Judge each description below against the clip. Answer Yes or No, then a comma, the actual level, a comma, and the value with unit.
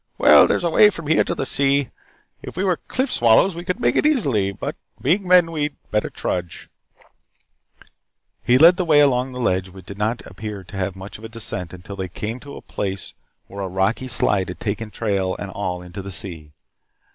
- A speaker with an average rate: No, fast, 215 wpm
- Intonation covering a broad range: Yes, wide, 7.4 semitones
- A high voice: No, low, 110 Hz